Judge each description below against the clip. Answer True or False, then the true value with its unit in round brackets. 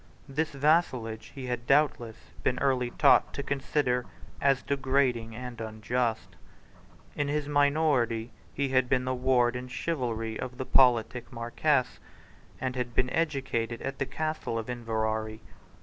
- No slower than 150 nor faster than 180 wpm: False (140 wpm)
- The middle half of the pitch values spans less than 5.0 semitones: True (2.9 semitones)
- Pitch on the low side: True (125 Hz)